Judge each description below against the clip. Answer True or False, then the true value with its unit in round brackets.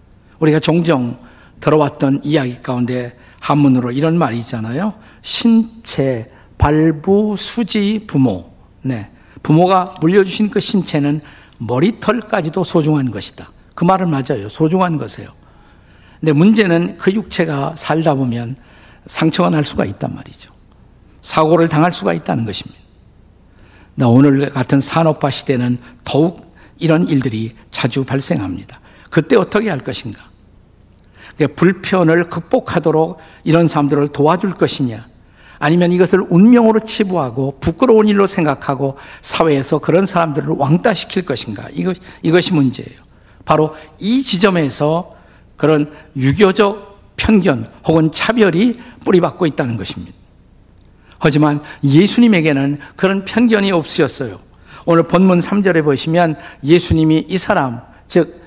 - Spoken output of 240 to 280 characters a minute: False (290 characters per minute)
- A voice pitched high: False (155 Hz)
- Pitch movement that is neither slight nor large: False (5.7 semitones)